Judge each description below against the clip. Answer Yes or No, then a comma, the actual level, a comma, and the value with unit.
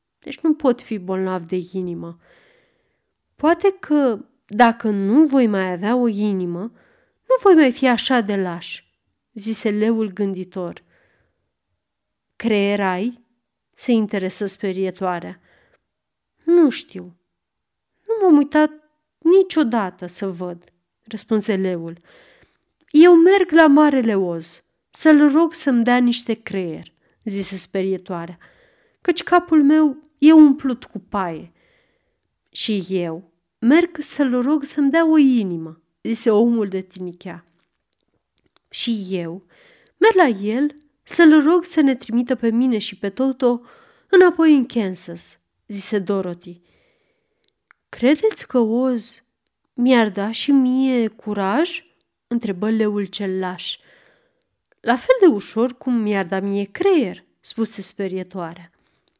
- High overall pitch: Yes, high, 235 Hz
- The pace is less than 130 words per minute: Yes, average, 120 wpm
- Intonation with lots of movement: Yes, wide, 8.0 semitones